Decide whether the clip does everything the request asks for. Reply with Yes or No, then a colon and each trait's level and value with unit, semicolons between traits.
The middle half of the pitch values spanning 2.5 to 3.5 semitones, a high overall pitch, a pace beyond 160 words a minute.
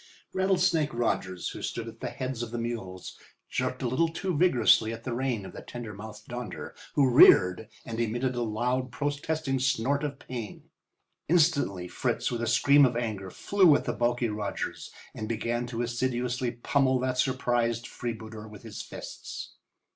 No: average, 3.1 semitones; low, 120 Hz; average, 170 wpm